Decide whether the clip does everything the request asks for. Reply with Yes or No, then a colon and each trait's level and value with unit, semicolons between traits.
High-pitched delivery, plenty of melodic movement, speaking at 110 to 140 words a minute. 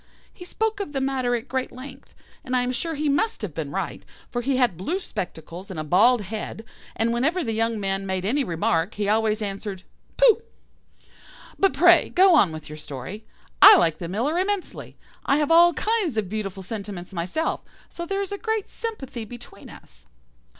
No: high, 235 Hz; wide, 8.8 semitones; average, 190 wpm